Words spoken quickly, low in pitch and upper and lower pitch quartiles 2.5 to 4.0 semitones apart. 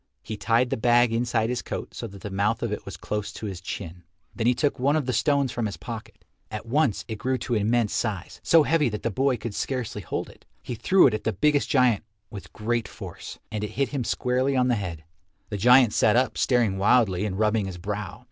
Yes: fast, 235 wpm; low, 115 Hz; average, 3.3 semitones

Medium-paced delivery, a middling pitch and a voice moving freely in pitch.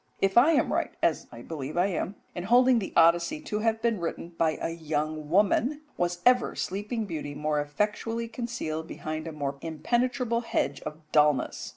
Yes: average, 180 wpm; medium, 175 Hz; wide, 6.7 semitones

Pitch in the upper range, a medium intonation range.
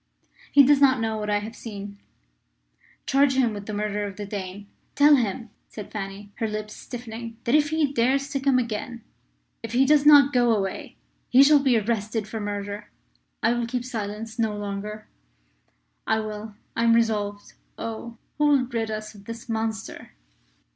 Yes: high, 225 Hz; average, 3.3 semitones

